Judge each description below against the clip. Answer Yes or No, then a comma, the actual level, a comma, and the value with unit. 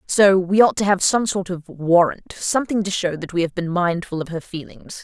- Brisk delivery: Yes, fast, 240 wpm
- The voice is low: No, medium, 185 Hz